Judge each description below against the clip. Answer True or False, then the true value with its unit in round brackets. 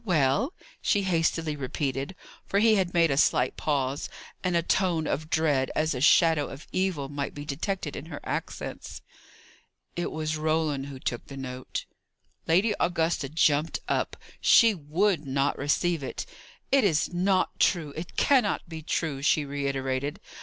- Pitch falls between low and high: True (155 Hz)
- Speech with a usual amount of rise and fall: True (3.8 semitones)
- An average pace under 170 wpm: True (155 wpm)